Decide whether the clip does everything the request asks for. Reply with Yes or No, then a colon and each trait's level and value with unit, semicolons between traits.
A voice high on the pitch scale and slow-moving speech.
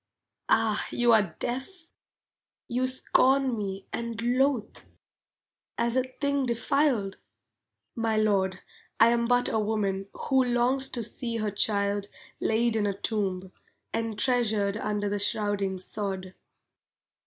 Yes: high, 225 Hz; slow, 120 wpm